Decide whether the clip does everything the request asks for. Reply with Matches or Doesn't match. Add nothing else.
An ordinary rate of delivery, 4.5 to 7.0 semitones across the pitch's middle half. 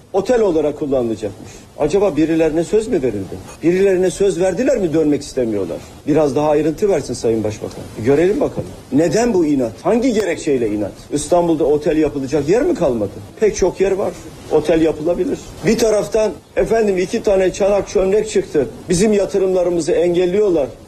Doesn't match